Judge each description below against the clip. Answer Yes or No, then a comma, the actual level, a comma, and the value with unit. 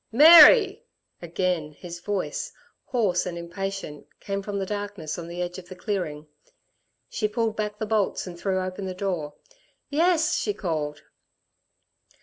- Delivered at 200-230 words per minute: No, average, 145 wpm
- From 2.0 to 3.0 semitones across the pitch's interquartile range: No, average, 3.6 semitones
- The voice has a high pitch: Yes, high, 195 Hz